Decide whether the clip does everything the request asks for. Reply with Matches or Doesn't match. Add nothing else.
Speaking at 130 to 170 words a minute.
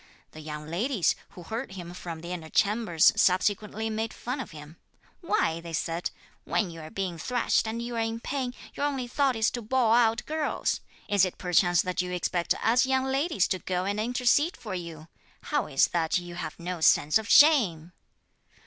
Doesn't match